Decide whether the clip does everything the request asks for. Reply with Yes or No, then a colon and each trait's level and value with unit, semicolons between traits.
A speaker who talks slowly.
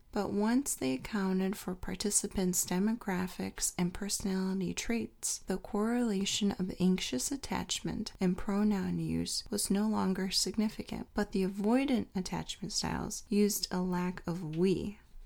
Yes: slow, 125 wpm